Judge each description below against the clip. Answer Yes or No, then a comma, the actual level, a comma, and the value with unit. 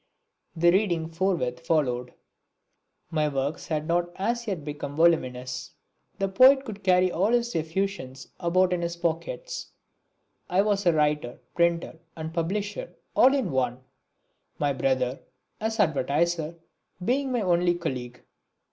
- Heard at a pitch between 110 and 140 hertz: No, medium, 170 Hz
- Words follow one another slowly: Yes, slow, 130 wpm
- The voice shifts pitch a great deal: No, average, 4.7 semitones